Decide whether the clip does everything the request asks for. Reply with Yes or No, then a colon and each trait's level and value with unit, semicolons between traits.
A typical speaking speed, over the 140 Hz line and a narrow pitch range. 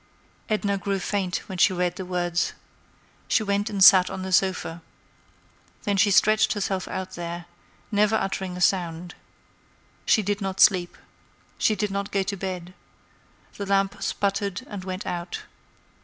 Yes: average, 155 wpm; high, 190 Hz; narrow, 2.0 semitones